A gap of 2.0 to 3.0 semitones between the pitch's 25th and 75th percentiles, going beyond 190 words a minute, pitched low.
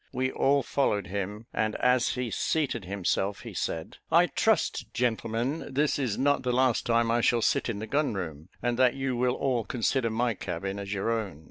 No: average, 4.1 semitones; average, 200 wpm; low, 115 Hz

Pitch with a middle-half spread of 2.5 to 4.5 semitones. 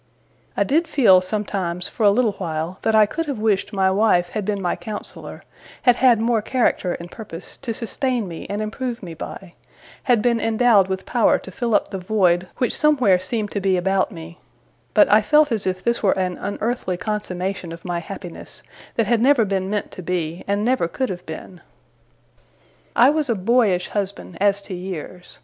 Yes: average, 4.1 semitones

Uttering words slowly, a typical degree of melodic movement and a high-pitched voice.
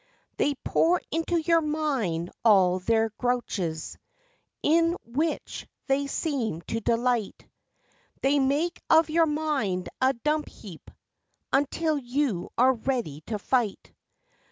No: slow, 115 wpm; wide, 5.7 semitones; very high, 265 Hz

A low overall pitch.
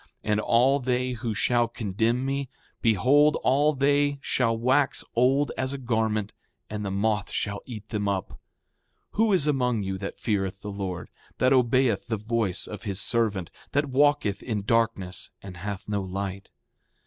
Yes: low, 115 Hz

